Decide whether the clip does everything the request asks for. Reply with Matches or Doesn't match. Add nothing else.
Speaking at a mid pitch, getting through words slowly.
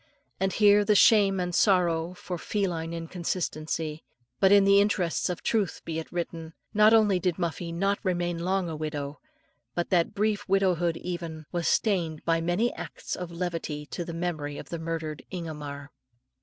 Doesn't match